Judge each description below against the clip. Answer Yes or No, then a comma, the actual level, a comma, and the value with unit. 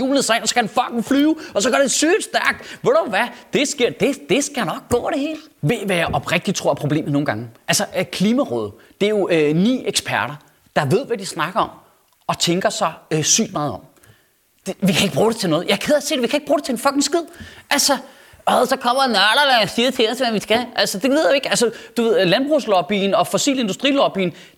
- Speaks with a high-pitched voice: Yes, high, 230 Hz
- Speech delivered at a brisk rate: Yes, fast, 250 wpm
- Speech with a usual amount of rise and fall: No, wide, 6.8 semitones